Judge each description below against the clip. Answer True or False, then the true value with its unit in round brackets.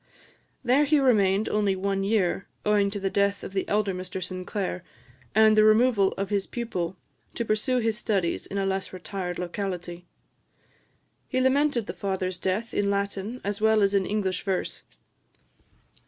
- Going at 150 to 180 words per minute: True (160 wpm)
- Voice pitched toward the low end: False (200 Hz)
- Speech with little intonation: True (2.3 semitones)